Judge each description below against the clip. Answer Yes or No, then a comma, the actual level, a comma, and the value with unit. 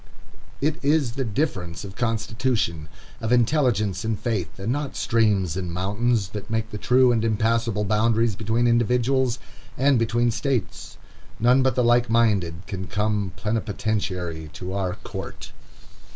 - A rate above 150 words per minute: No, average, 140 wpm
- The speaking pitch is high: No, low, 110 Hz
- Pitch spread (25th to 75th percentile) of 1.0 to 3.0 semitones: No, average, 3.5 semitones